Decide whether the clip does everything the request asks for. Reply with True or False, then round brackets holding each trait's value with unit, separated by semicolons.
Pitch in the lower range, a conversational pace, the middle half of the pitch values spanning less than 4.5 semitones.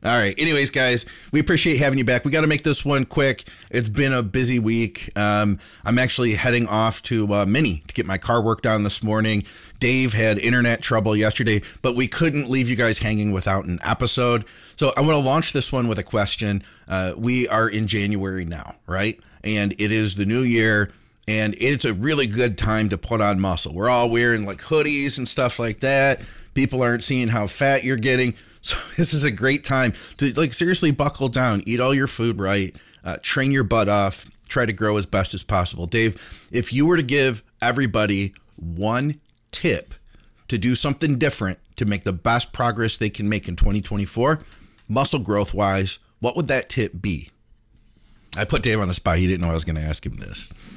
False (115 Hz; 210 wpm; 4.0 semitones)